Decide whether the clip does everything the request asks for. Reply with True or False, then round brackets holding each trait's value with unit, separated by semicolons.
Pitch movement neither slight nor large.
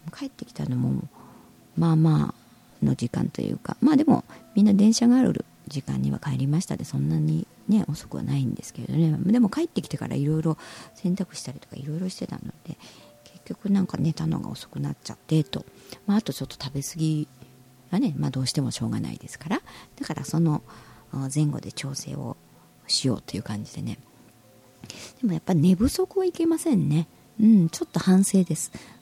False (7.1 semitones)